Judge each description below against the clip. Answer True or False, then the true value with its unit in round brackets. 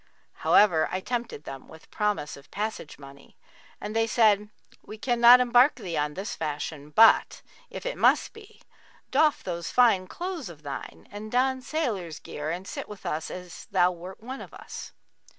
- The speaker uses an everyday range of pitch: False (6.8 semitones)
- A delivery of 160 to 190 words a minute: True (170 wpm)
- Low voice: False (205 Hz)